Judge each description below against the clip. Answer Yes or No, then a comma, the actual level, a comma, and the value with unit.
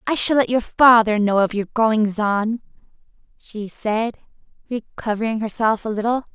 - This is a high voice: Yes, high, 220 Hz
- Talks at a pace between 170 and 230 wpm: No, average, 150 wpm